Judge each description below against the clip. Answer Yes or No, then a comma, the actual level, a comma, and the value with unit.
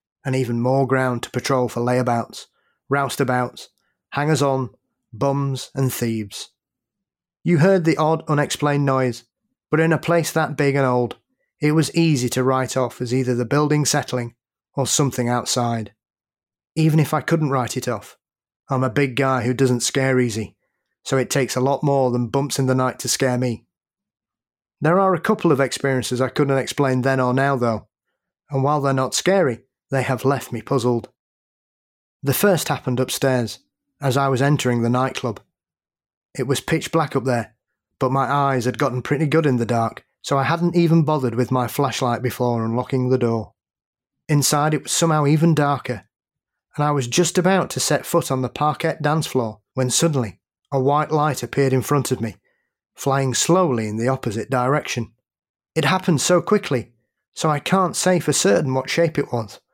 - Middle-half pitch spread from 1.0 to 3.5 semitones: Yes, average, 3.1 semitones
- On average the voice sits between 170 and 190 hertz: No, low, 135 Hz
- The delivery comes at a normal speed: Yes, average, 180 wpm